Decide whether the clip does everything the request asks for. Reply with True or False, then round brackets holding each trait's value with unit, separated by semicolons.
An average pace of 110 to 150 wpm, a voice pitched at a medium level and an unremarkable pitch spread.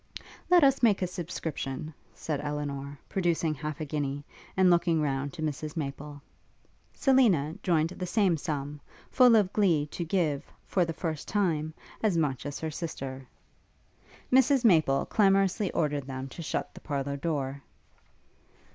True (145 wpm; 155 Hz; 4.3 semitones)